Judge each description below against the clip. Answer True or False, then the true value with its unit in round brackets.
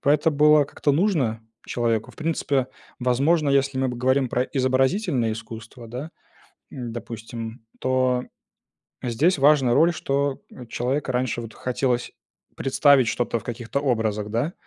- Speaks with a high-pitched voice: False (130 Hz)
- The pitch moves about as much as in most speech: True (3.1 semitones)